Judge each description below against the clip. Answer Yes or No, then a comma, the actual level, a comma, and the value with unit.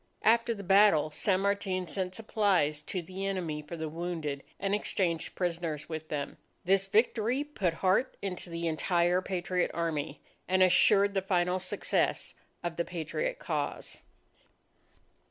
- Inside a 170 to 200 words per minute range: No, average, 140 wpm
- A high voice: No, medium, 180 Hz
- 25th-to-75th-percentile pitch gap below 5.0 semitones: Yes, average, 3.1 semitones